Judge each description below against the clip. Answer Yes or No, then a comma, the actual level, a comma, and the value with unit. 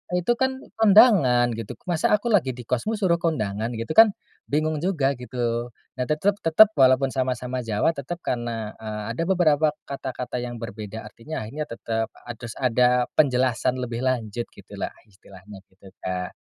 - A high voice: No, low, 125 Hz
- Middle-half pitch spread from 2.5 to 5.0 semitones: No, wide, 5.4 semitones